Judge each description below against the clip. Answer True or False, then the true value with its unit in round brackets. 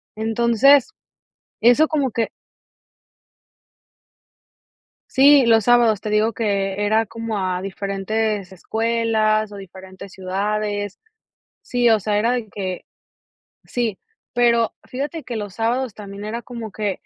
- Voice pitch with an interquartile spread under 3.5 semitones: True (2.7 semitones)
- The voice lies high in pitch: True (220 Hz)